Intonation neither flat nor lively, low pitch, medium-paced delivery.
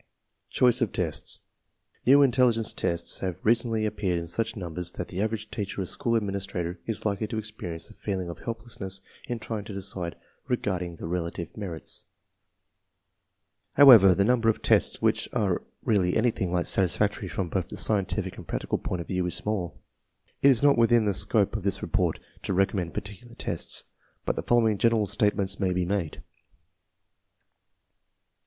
Yes: average, 3.8 semitones; low, 100 Hz; average, 165 wpm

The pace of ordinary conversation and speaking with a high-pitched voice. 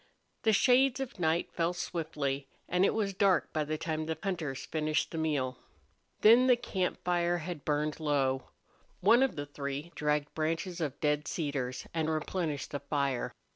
No: average, 170 wpm; medium, 160 Hz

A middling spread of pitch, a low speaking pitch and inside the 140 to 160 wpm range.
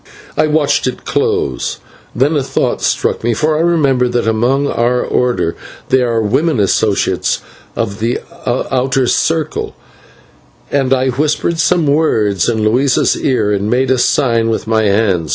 Yes: average, 4.2 semitones; low, 125 Hz; average, 155 wpm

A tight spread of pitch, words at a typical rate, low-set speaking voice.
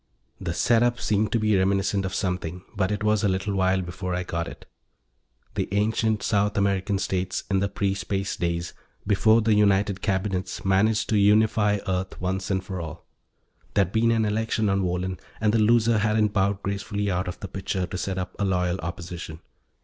Yes: narrow, 2.1 semitones; average, 190 wpm; low, 100 Hz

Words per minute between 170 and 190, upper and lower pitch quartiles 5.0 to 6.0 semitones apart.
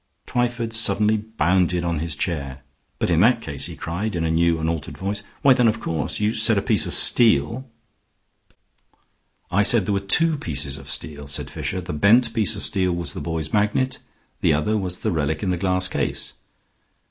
No: average, 200 wpm; average, 5.3 semitones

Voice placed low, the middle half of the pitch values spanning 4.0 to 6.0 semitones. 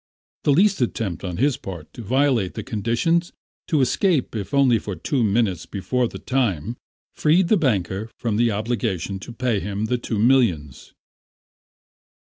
Yes: low, 115 Hz; average, 5.0 semitones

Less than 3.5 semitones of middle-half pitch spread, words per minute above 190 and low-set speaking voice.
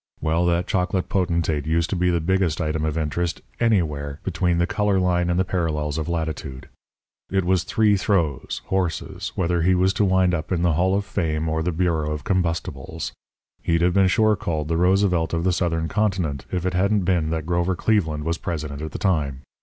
Yes: average, 2.8 semitones; average, 200 wpm; very low, 85 Hz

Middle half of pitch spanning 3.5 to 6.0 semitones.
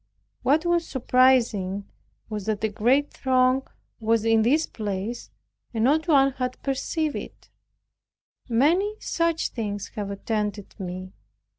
Yes: average, 4.9 semitones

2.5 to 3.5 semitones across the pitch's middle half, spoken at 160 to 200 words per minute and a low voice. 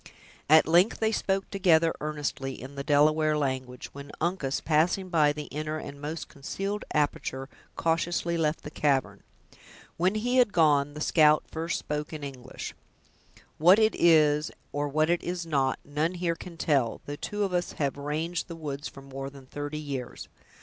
No: average, 3.2 semitones; average, 170 wpm; medium, 155 Hz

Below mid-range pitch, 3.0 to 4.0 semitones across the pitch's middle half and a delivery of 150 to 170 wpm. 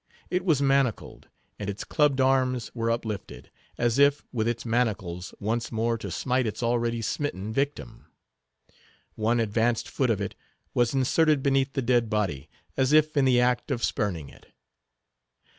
Yes: low, 120 Hz; average, 3.5 semitones; average, 160 wpm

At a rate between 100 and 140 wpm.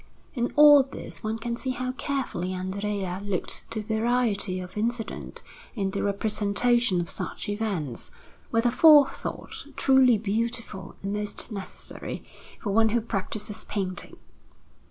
Yes: slow, 135 wpm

